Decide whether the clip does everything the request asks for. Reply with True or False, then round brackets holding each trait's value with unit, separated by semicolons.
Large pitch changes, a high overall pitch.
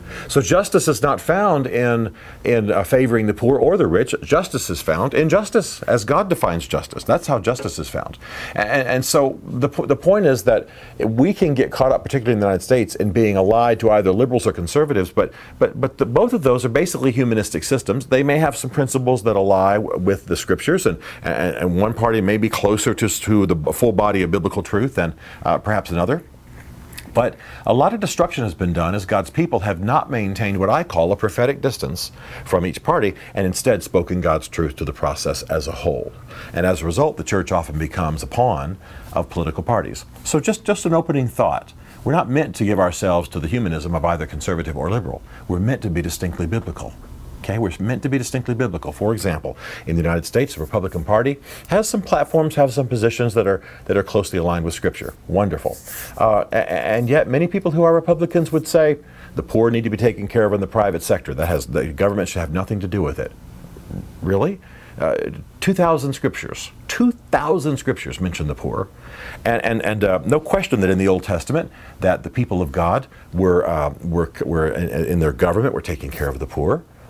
False (6.9 semitones; 105 Hz)